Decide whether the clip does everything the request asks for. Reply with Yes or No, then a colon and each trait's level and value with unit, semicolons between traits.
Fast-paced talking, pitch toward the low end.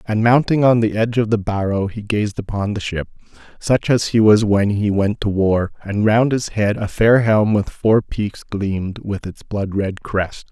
Yes: fast, 215 wpm; low, 105 Hz